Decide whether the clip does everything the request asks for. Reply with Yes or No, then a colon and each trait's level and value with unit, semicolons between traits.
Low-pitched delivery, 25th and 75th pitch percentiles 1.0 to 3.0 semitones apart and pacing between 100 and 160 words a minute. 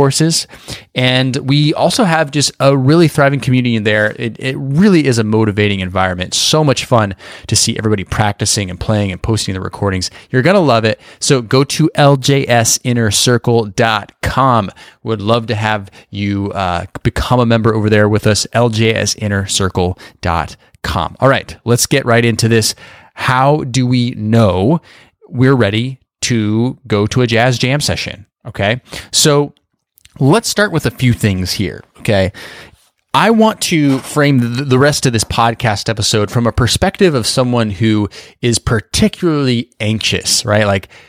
No: low, 115 Hz; average, 4.2 semitones; average, 155 wpm